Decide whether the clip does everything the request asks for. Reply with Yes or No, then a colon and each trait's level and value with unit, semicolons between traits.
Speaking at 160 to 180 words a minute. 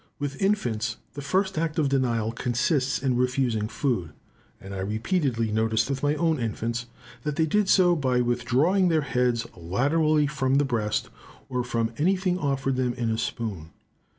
Yes: average, 165 wpm